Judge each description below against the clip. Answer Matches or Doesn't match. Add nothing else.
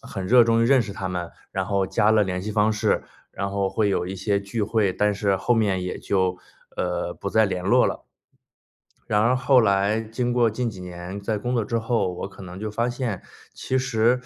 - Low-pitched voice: Matches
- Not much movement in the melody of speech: Doesn't match